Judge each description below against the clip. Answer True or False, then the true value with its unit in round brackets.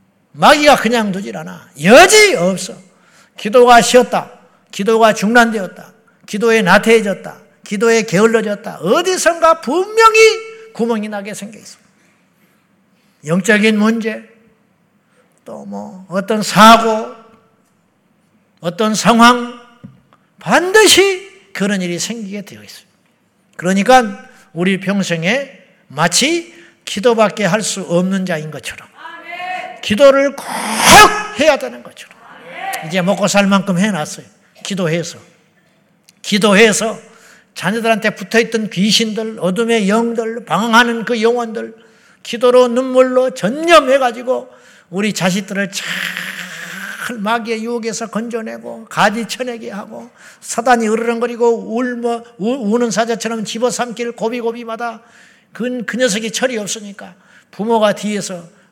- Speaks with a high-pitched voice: True (225 Hz)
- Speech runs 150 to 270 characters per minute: True (250 characters per minute)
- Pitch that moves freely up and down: False (3.2 semitones)